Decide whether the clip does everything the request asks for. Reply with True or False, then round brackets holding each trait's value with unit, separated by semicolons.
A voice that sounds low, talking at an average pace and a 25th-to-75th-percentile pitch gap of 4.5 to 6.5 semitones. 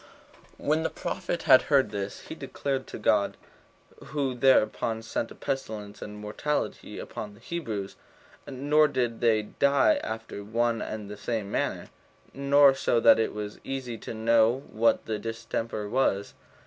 False (115 Hz; 160 wpm; 4.0 semitones)